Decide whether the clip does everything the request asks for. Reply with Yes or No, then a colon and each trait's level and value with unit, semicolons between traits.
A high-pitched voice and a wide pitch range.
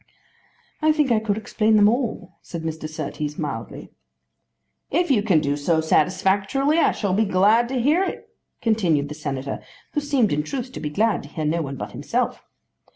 Yes: high, 195 Hz; wide, 7.6 semitones